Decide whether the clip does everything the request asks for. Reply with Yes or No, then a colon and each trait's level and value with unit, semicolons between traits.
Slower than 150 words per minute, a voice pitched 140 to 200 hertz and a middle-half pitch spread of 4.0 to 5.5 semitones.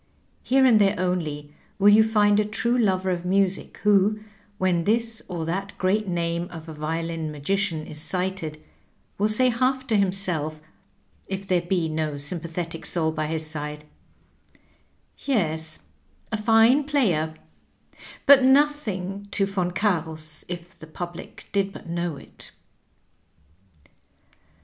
Yes: slow, 135 wpm; medium, 185 Hz; average, 4.5 semitones